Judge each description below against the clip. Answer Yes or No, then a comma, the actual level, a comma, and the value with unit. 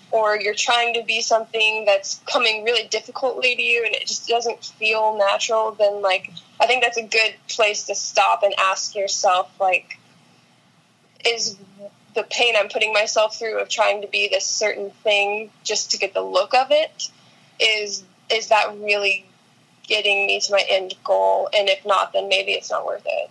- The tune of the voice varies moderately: No, narrow, 2.3 semitones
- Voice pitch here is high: Yes, high, 215 Hz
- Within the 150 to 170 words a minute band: No, average, 185 wpm